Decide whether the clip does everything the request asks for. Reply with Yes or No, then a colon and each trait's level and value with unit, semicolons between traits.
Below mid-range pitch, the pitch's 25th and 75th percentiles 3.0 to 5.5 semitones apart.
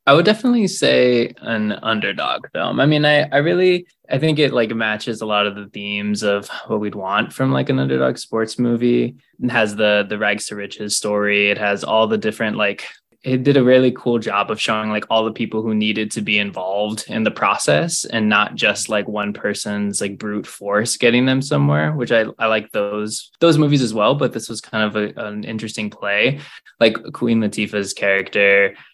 No: low, 110 Hz; narrow, 2.6 semitones